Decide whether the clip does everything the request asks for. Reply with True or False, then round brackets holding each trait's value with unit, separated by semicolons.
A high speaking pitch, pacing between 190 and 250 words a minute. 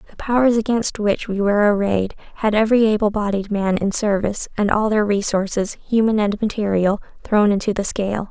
False (210 Hz; 180 wpm)